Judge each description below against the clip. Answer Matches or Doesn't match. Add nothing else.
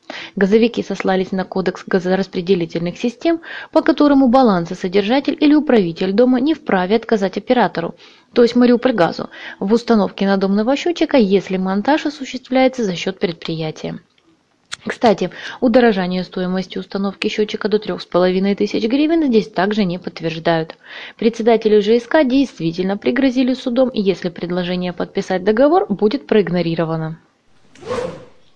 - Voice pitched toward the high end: Matches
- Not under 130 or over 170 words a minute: Doesn't match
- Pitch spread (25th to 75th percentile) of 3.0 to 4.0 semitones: Doesn't match